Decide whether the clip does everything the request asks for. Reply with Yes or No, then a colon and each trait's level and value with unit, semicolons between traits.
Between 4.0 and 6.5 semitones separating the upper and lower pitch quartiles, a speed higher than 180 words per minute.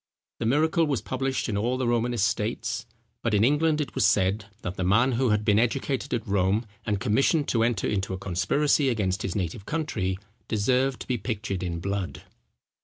Yes: average, 4.5 semitones; average, 190 wpm